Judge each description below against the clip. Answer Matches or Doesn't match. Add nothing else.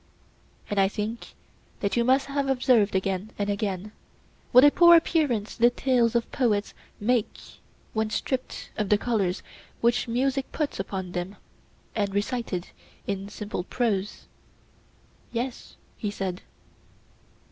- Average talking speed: Doesn't match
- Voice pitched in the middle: Doesn't match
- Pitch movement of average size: Matches